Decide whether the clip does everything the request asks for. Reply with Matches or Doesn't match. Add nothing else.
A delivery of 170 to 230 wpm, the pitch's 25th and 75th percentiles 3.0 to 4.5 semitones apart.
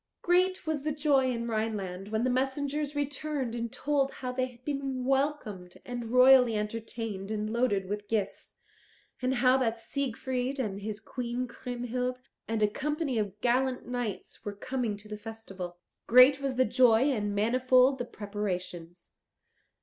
Doesn't match